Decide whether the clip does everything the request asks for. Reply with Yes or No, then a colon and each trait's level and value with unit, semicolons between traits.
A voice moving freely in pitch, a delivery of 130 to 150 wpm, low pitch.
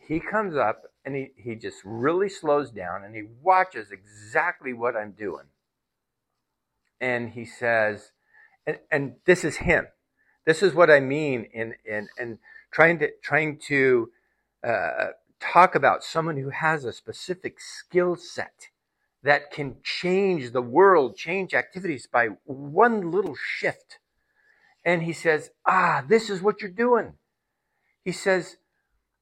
No: wide, 7.2 semitones; average, 140 wpm; medium, 160 Hz